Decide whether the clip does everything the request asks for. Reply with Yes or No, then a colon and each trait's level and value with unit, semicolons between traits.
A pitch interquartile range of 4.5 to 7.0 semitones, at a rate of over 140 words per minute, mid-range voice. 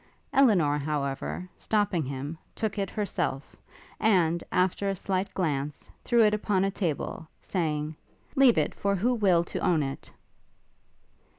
No: average, 5.3 semitones; slow, 135 wpm; medium, 180 Hz